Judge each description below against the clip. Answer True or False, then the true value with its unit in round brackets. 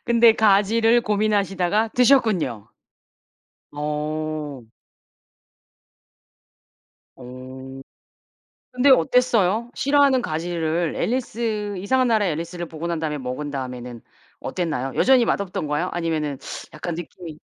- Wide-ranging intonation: True (6.9 semitones)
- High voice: False (175 Hz)